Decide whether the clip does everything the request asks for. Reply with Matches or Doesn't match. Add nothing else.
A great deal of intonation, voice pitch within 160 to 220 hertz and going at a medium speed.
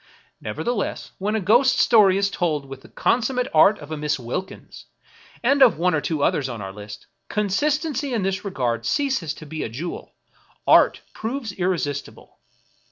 Matches